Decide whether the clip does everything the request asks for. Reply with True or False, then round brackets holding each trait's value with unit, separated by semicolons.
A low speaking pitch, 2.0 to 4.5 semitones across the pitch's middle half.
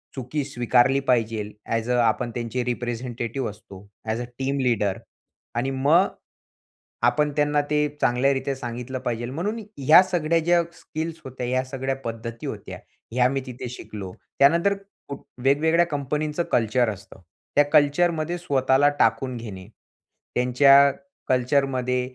True (130 Hz; 3.4 semitones)